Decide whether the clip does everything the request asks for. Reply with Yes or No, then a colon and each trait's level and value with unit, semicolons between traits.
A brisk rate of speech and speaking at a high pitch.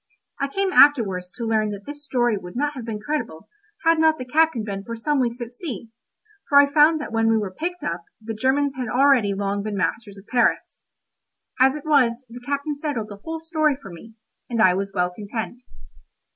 Yes: fast, 210 wpm; high, 240 Hz